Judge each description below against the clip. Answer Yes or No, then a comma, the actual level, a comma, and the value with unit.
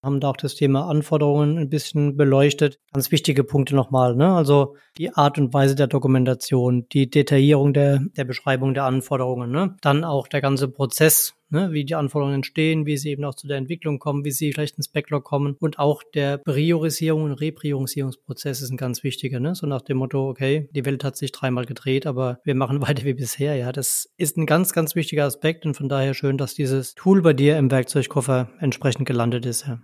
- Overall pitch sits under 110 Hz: No, medium, 140 Hz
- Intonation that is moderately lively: No, narrow, 1.8 semitones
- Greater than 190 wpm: Yes, fast, 210 wpm